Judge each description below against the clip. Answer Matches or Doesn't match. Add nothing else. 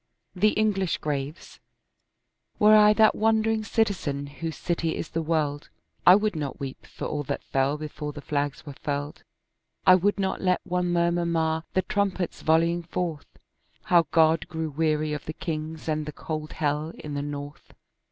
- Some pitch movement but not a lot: Matches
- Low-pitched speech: Doesn't match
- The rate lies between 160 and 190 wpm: Matches